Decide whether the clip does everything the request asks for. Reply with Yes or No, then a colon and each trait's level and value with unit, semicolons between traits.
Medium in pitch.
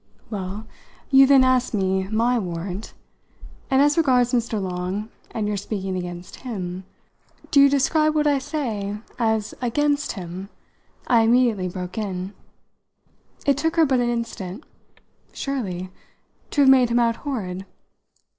No: high, 225 Hz